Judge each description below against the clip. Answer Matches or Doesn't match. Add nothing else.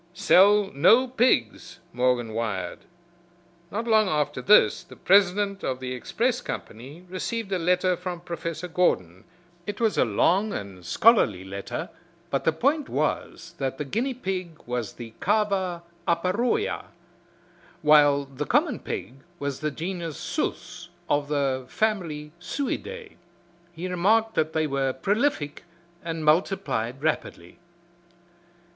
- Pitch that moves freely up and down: Matches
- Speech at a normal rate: Doesn't match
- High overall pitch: Doesn't match